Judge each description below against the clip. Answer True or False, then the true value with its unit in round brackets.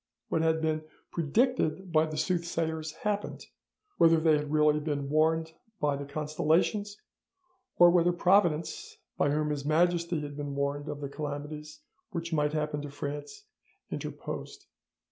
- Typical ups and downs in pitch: False (2.3 semitones)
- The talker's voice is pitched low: False (155 Hz)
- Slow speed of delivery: False (145 wpm)